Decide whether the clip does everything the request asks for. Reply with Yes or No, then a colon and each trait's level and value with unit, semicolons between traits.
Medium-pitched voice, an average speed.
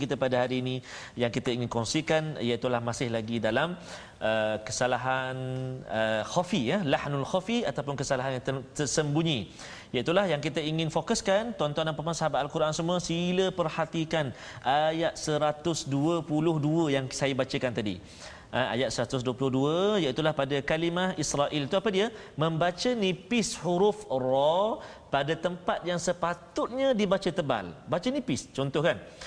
No: medium, 155 Hz; fast, 140 wpm